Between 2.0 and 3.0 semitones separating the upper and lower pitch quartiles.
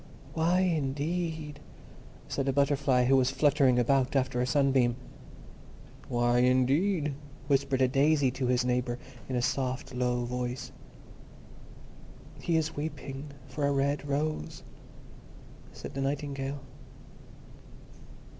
Yes: narrow, 2.5 semitones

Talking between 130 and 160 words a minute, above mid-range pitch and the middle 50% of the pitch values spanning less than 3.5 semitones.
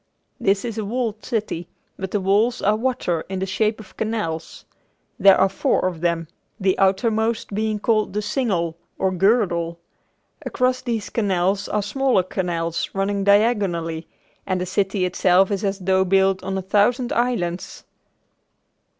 Yes: average, 150 wpm; high, 195 Hz; average, 2.9 semitones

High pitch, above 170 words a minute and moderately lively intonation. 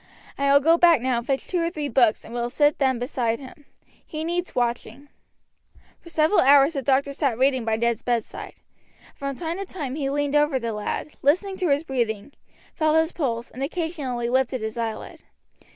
Yes: very high, 275 Hz; average, 195 wpm; average, 4.4 semitones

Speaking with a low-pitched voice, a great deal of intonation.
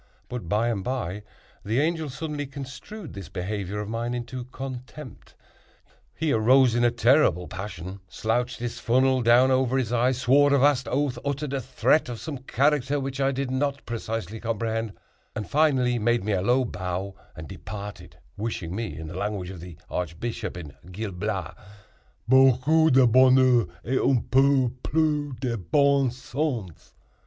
No: low, 125 Hz; average, 4.2 semitones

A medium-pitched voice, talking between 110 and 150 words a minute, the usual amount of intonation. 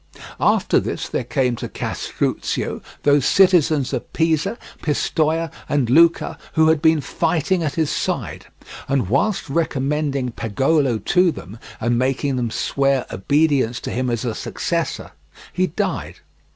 Yes: medium, 145 Hz; average, 140 wpm; average, 4.1 semitones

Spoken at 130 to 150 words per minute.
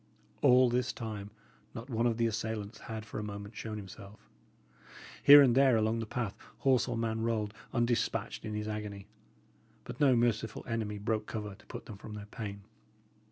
No: average, 180 wpm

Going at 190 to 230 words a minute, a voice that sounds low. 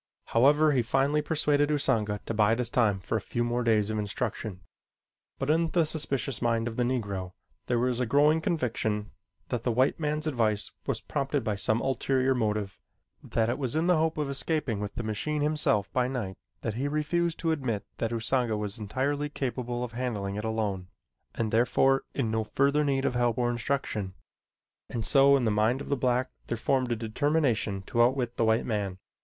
Yes: average, 195 wpm; low, 120 Hz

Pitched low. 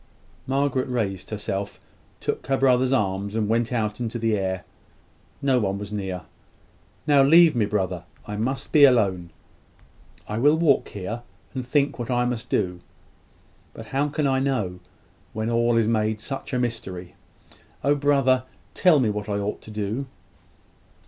Yes: low, 115 Hz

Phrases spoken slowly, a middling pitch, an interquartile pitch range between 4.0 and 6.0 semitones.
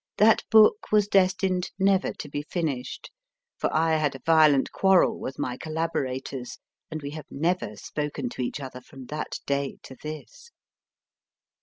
No: average, 155 wpm; medium, 155 Hz; average, 5.2 semitones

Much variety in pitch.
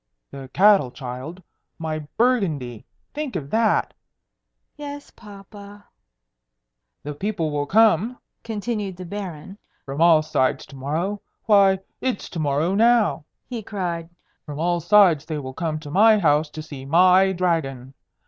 Yes: wide, 5.7 semitones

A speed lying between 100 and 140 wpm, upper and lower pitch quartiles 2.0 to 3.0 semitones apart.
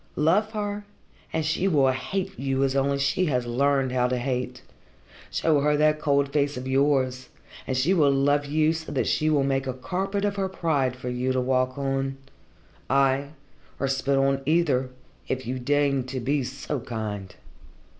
No: average, 180 wpm; average, 2.7 semitones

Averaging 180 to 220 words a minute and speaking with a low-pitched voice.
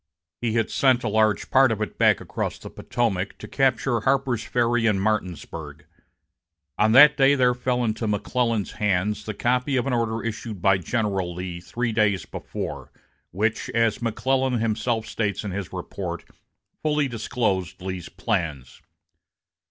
No: average, 150 wpm; low, 110 Hz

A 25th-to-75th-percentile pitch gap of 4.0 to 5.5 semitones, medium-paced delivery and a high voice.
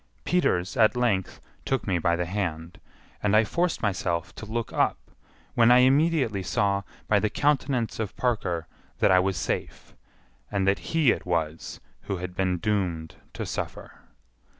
No: average, 5.2 semitones; average, 160 wpm; low, 100 Hz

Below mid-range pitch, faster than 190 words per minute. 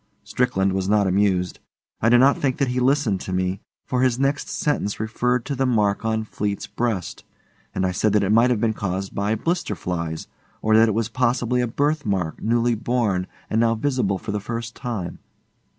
Yes: low, 110 Hz; average, 200 wpm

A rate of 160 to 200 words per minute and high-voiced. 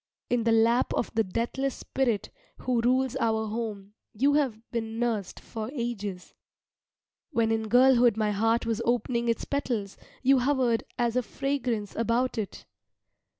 No: average, 150 wpm; high, 235 Hz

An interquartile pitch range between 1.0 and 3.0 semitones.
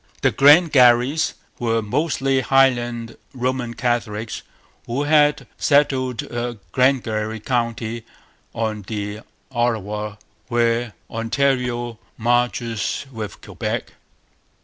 Yes: average, 2.7 semitones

